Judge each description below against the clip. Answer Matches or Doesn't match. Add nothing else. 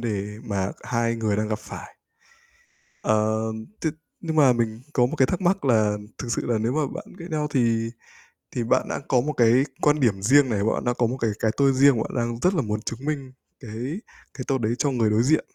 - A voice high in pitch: Doesn't match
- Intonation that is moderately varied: Matches